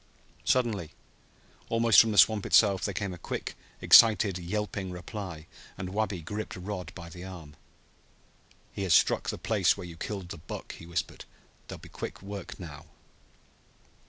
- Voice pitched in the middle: No, very low, 95 Hz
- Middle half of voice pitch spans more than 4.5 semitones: No, average, 3.1 semitones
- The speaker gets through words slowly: No, average, 160 wpm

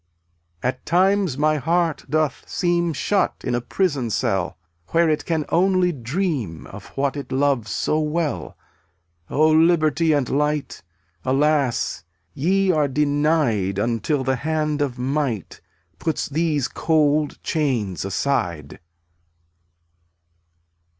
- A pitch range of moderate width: Yes, average, 3.9 semitones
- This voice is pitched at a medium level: Yes, medium, 150 Hz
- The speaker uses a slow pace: Yes, slow, 115 wpm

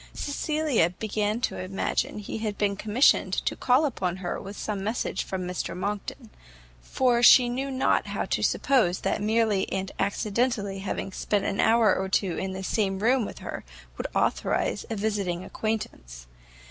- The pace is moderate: Yes, average, 165 wpm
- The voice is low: No, high, 205 Hz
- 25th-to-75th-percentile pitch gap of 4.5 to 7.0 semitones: No, average, 3.4 semitones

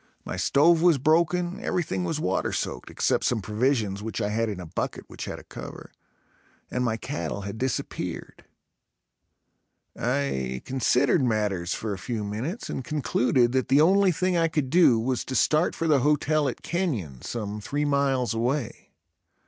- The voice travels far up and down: Yes, wide, 5.9 semitones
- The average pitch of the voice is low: Yes, low, 130 Hz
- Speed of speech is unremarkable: Yes, average, 165 wpm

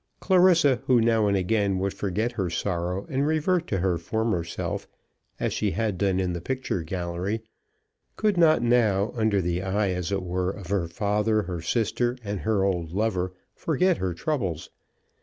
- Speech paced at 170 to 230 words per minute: Yes, average, 175 wpm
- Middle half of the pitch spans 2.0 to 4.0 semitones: No, average, 4.4 semitones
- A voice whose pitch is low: Yes, low, 100 Hz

